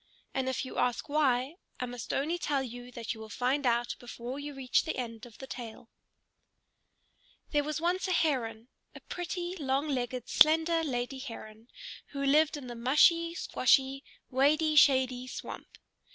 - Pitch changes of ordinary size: Yes, average, 3.7 semitones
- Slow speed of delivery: No, average, 165 wpm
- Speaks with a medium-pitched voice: No, very high, 265 Hz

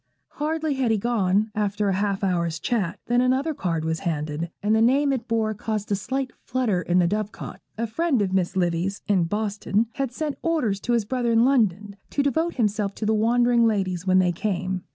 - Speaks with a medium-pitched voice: No, high, 215 Hz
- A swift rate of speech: Yes, fast, 210 wpm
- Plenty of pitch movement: No, average, 4.4 semitones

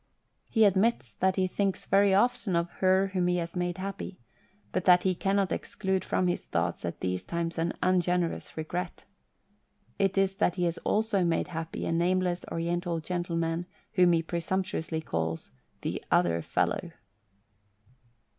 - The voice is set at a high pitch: No, medium, 180 Hz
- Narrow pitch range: Yes, narrow, 2.2 semitones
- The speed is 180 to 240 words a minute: No, average, 160 wpm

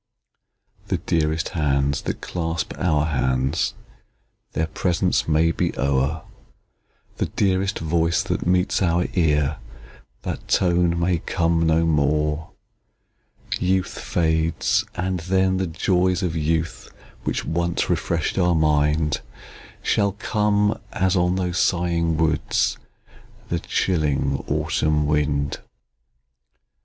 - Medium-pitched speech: No, very low, 85 Hz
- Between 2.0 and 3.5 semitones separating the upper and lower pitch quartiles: Yes, average, 2.9 semitones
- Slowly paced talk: Yes, slow, 110 wpm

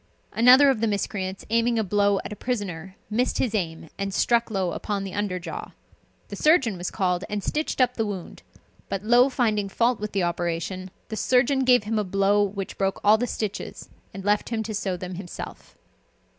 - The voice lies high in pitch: Yes, high, 205 Hz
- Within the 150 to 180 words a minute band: No, average, 200 wpm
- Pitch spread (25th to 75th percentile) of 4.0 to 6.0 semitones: No, average, 3.4 semitones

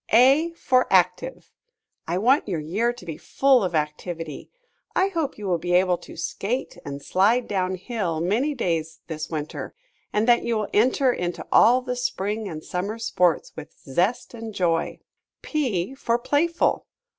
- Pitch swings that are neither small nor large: No, wide, 6.3 semitones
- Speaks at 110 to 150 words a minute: No, average, 165 wpm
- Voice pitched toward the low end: No, high, 200 Hz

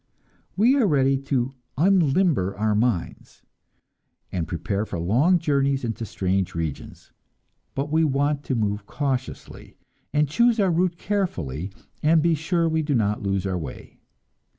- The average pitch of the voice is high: No, low, 135 Hz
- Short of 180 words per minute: Yes, average, 145 wpm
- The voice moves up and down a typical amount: No, wide, 8.2 semitones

